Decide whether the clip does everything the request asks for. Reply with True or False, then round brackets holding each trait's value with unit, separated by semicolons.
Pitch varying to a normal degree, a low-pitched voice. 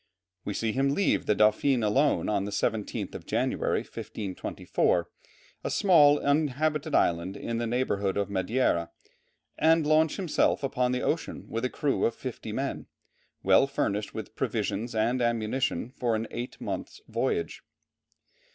True (5.0 semitones; 120 Hz)